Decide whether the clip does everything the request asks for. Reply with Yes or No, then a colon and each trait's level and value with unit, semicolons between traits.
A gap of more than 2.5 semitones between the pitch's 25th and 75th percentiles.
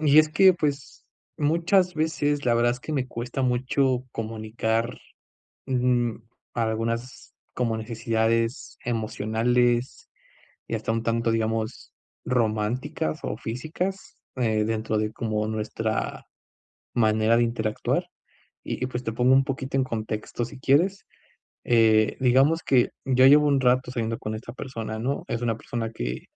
Yes: average, 2.9 semitones